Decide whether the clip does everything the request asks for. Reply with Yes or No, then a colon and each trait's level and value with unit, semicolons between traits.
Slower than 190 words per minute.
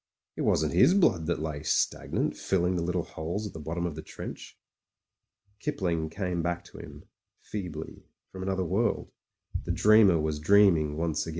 Yes: average, 175 wpm